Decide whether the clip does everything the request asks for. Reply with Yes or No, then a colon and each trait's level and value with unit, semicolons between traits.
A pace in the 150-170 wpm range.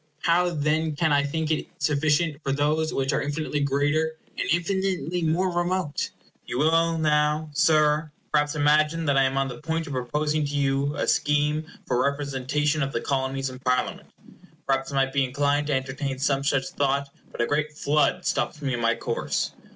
No: average, 190 wpm